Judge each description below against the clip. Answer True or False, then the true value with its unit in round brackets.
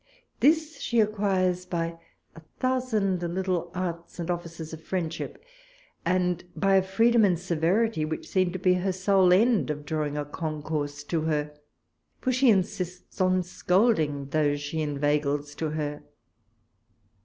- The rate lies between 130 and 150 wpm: True (145 wpm)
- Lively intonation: False (3.8 semitones)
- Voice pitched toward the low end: False (175 Hz)